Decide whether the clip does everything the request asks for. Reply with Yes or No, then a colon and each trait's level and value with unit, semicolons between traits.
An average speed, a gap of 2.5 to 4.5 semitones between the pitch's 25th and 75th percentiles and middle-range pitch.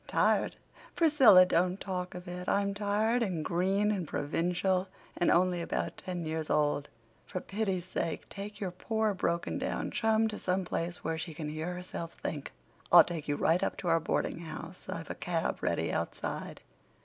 Yes: average, 175 wpm; average, 3.1 semitones; medium, 180 Hz